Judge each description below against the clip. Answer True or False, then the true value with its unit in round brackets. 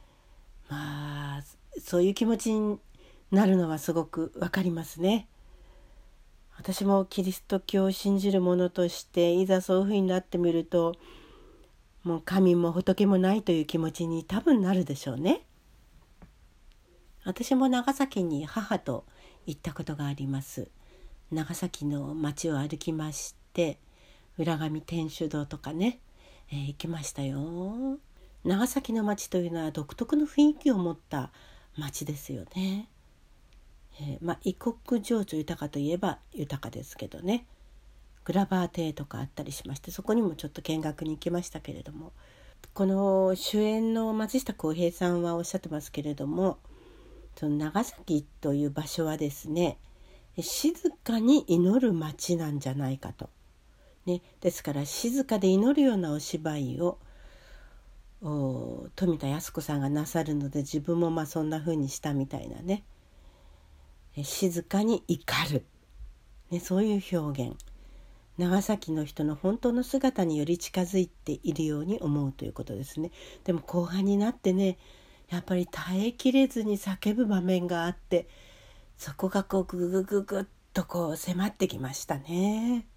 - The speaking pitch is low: False (170 Hz)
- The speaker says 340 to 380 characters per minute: False (280 characters per minute)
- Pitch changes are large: False (4.7 semitones)